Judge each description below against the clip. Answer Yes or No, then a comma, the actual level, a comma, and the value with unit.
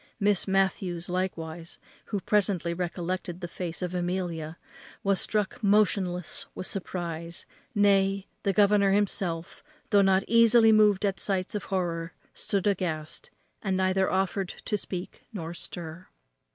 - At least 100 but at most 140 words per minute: Yes, slow, 135 wpm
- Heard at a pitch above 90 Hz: Yes, medium, 185 Hz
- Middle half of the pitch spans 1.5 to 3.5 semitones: Yes, narrow, 2.4 semitones